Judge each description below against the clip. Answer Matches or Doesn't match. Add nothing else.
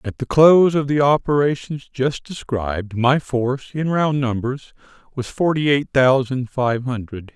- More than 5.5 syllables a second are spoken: Doesn't match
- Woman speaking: Doesn't match